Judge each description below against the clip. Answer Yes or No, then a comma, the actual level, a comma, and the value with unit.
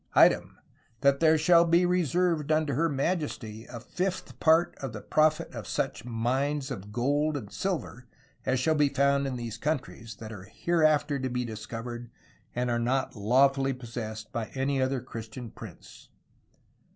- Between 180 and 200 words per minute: No, average, 165 wpm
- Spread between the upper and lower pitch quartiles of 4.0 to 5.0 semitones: Yes, average, 4.6 semitones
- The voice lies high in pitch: No, low, 135 Hz